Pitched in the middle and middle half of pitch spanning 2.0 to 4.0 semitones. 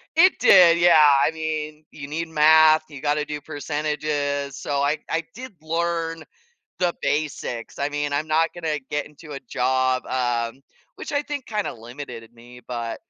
Yes: medium, 150 Hz; average, 2.7 semitones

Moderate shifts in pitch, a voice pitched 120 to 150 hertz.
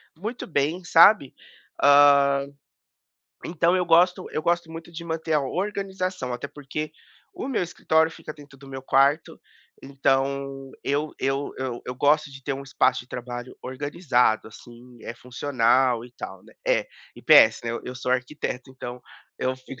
Yes: average, 4.0 semitones; medium, 140 Hz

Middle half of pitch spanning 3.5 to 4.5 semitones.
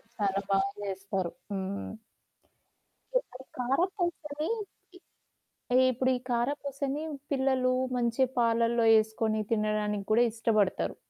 Yes: average, 4.2 semitones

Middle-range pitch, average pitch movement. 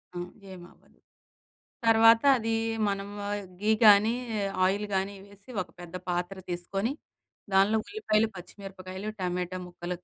No: high, 195 Hz; average, 3.0 semitones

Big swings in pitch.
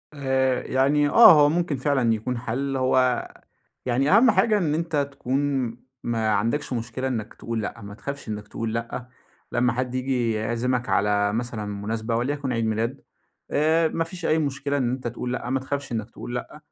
No: average, 3.6 semitones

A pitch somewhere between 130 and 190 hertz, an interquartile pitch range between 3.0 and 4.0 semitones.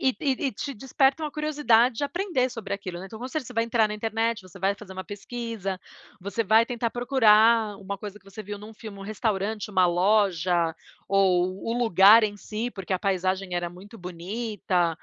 No: high, 210 Hz; average, 3.4 semitones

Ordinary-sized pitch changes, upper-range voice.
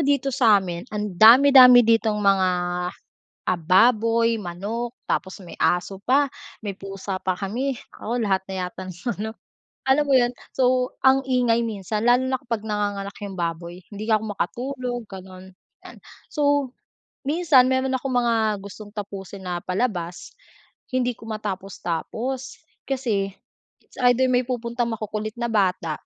Yes: average, 4.4 semitones; high, 220 Hz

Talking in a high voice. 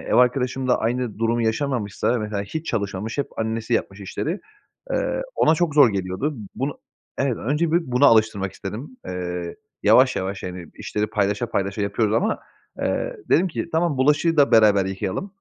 No: low, 115 Hz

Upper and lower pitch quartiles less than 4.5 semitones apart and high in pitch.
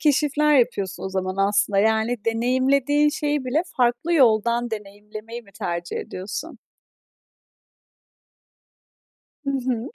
No: average, 4.9 semitones; high, 240 Hz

